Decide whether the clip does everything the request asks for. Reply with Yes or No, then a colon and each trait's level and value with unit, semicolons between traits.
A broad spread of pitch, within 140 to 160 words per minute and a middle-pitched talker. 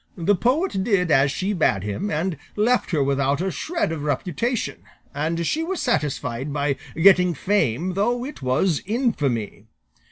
Yes: wide, 6.5 semitones; average, 155 wpm; medium, 170 Hz